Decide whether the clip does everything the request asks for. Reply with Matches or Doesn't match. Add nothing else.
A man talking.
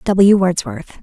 Doesn't match